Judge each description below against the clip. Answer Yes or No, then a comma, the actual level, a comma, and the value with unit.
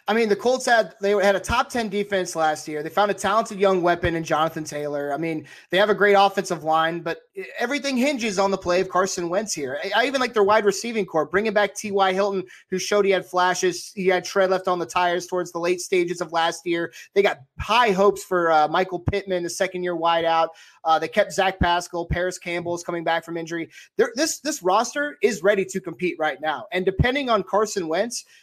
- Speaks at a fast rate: Yes, fast, 230 wpm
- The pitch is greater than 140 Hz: Yes, medium, 185 Hz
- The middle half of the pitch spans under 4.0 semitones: Yes, average, 3.3 semitones